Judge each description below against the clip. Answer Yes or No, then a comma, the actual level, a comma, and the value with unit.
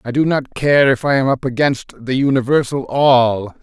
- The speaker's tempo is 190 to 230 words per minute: Yes, average, 200 wpm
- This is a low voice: Yes, low, 130 Hz